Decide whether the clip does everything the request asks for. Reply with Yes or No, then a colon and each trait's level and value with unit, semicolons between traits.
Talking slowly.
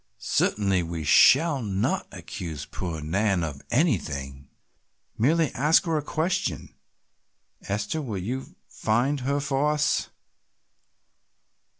Yes: slow, 105 wpm